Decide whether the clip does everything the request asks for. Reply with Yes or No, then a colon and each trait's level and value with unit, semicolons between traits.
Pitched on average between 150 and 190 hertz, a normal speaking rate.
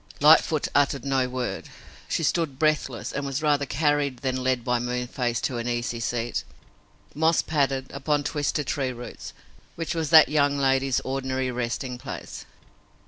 No: low, 135 Hz; average, 150 wpm